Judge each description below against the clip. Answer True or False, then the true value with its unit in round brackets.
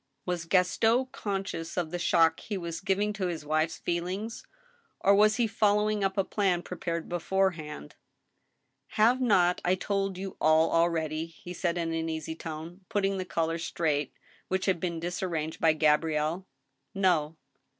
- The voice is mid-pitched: True (175 Hz)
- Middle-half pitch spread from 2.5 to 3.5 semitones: True (3.1 semitones)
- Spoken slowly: False (165 wpm)